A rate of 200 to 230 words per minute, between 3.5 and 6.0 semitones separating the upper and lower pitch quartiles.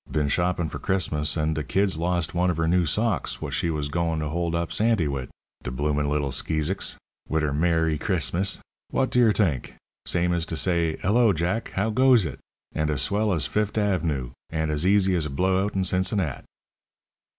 Yes: fast, 205 wpm; average, 3.8 semitones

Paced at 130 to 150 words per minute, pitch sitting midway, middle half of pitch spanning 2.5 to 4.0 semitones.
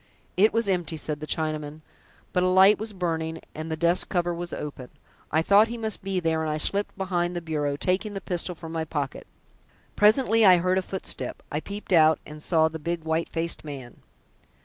No: fast, 205 wpm; medium, 170 Hz; average, 3.2 semitones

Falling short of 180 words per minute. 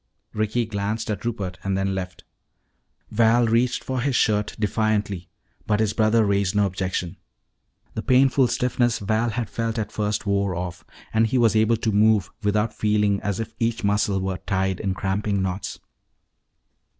Yes: average, 160 wpm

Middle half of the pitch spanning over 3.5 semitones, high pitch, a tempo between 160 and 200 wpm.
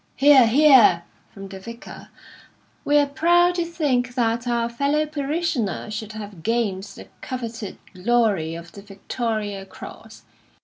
No: wide, 5.6 semitones; high, 235 Hz; slow, 135 wpm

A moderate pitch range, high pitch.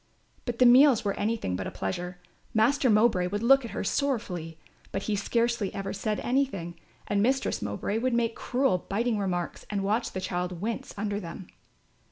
Yes: average, 4.5 semitones; high, 210 Hz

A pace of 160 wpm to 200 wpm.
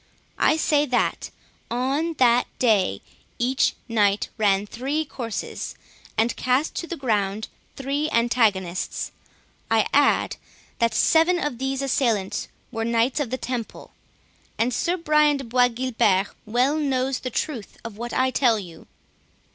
No: slow, 135 wpm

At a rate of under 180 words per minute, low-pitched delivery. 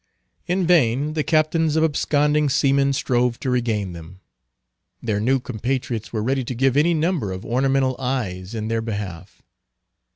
Yes: average, 155 wpm; low, 130 Hz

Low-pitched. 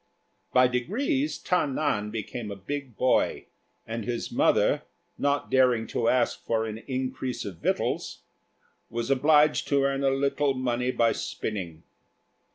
Yes: low, 130 Hz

